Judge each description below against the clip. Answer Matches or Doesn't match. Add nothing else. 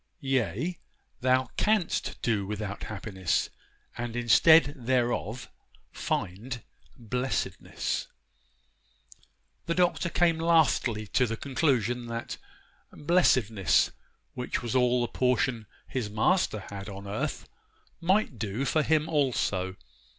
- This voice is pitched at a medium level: Doesn't match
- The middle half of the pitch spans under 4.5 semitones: Doesn't match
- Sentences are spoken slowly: Matches